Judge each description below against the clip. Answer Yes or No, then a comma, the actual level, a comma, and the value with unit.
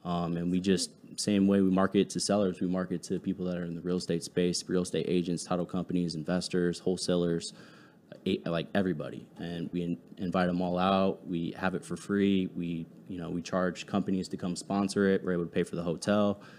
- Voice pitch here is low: Yes, very low, 90 Hz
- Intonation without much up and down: Yes, narrow, 1.6 semitones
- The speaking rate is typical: No, fast, 210 wpm